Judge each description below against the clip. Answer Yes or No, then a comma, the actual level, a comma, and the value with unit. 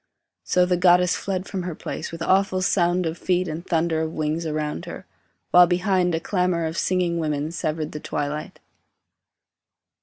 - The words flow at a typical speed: Yes, average, 170 wpm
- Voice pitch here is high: No, medium, 170 Hz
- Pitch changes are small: Yes, narrow, 2.3 semitones